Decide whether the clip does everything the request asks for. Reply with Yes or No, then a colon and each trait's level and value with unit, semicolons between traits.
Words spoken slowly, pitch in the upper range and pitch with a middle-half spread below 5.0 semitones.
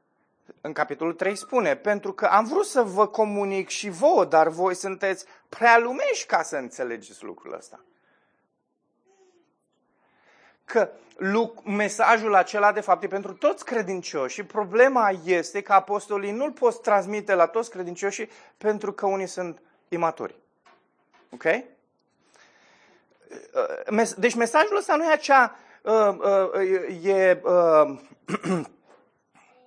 Yes: slow, 110 wpm; high, 210 Hz; average, 4.3 semitones